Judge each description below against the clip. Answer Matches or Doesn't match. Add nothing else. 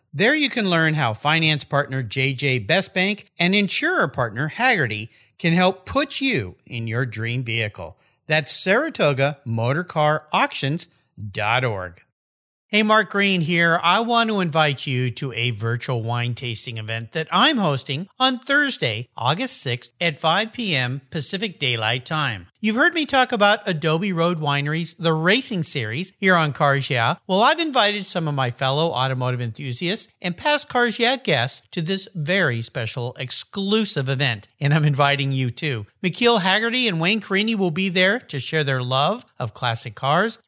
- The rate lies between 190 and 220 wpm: Doesn't match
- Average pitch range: Doesn't match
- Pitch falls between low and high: Matches